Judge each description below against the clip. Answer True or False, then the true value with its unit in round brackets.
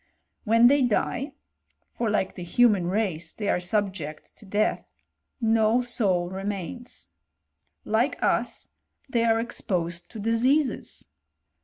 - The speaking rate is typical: False (120 wpm)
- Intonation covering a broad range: False (4.2 semitones)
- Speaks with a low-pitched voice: False (215 Hz)